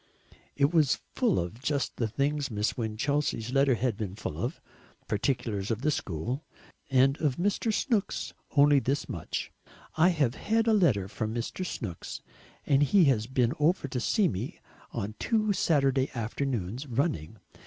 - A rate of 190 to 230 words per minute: No, average, 155 wpm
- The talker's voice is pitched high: No, low, 135 Hz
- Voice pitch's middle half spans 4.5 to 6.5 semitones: Yes, average, 5.0 semitones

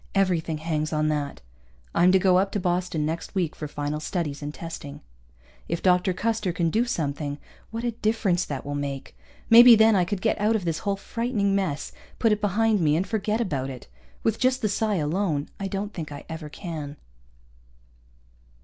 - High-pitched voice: No, medium, 180 Hz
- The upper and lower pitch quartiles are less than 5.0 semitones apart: No, wide, 5.5 semitones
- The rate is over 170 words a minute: Yes, average, 190 wpm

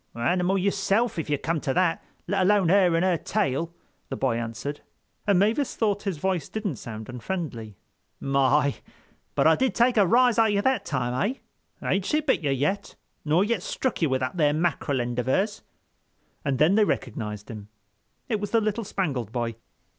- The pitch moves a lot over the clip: Yes, wide, 7.5 semitones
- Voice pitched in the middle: Yes, medium, 170 Hz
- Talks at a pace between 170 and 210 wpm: Yes, average, 190 wpm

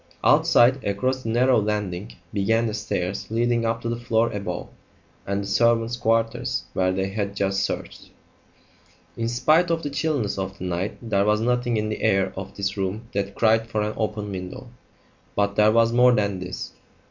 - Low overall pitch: Yes, low, 110 Hz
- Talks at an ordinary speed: Yes, average, 180 wpm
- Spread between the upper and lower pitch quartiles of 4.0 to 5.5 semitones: No, average, 2.9 semitones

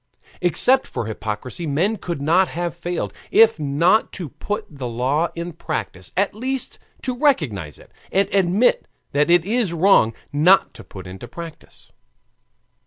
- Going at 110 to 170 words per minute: Yes, average, 155 wpm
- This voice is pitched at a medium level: Yes, medium, 170 Hz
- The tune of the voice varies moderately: No, wide, 6.0 semitones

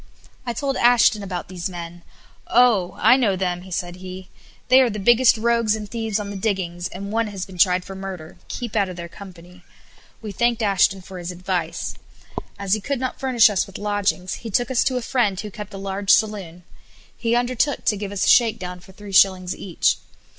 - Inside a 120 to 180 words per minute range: No, fast, 205 wpm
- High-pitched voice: Yes, high, 200 Hz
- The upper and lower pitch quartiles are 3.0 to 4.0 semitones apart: Yes, average, 3.7 semitones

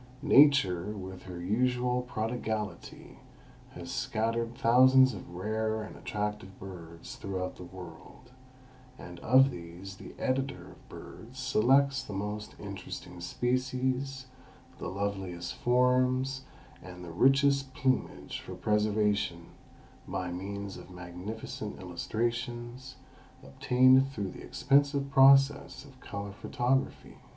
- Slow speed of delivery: Yes, slow, 110 wpm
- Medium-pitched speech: No, low, 110 Hz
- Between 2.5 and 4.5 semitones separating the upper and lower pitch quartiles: No, average, 5.2 semitones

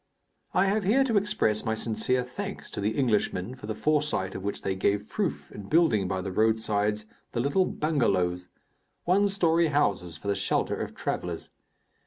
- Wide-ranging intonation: Yes, wide, 8.4 semitones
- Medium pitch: No, low, 110 Hz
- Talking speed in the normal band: Yes, average, 175 wpm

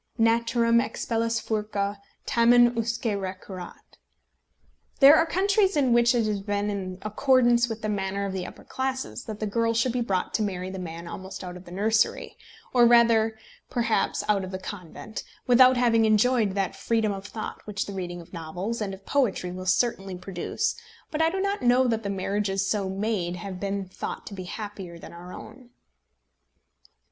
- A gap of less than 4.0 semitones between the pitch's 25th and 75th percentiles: Yes, average, 3.6 semitones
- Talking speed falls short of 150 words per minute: No, average, 180 wpm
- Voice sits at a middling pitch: No, high, 215 Hz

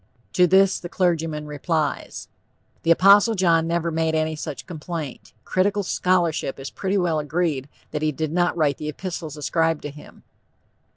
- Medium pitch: Yes, medium, 165 Hz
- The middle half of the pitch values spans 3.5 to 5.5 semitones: No, average, 2.9 semitones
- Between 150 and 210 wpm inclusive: Yes, average, 160 wpm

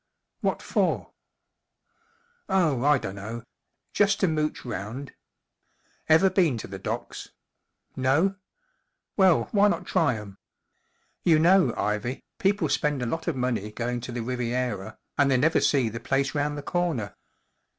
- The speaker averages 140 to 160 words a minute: Yes, average, 150 wpm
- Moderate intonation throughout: No, wide, 5.9 semitones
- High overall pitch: No, low, 135 Hz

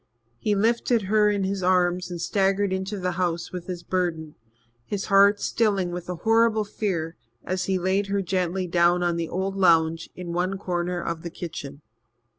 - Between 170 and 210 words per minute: Yes, average, 180 wpm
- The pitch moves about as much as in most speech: No, narrow, 2.3 semitones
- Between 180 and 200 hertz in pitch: Yes, medium, 185 Hz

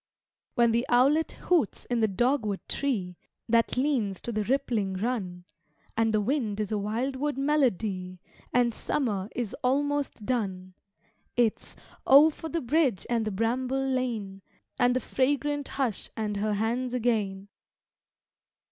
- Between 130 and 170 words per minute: Yes, average, 140 wpm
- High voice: Yes, high, 235 Hz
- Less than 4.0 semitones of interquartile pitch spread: No, average, 4.4 semitones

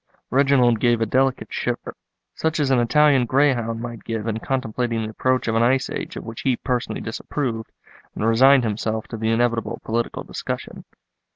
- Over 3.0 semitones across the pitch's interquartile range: No, narrow, 2.6 semitones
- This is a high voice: No, low, 120 Hz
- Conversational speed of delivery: Yes, average, 175 wpm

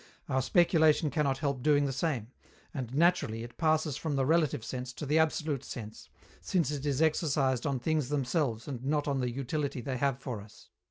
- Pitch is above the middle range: No, medium, 140 Hz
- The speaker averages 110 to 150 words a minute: No, average, 195 wpm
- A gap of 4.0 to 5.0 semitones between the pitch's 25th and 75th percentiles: No, average, 3.4 semitones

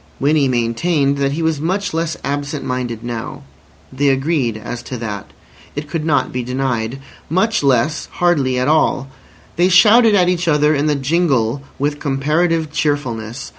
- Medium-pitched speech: Yes, medium, 145 Hz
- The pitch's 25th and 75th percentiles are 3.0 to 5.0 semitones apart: Yes, average, 4.2 semitones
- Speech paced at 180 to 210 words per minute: No, average, 155 wpm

